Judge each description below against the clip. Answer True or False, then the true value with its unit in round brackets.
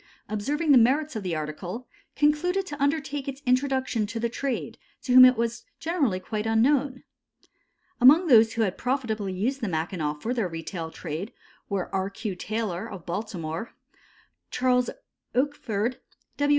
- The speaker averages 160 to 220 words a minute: False (150 wpm)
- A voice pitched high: True (230 Hz)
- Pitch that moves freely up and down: True (5.7 semitones)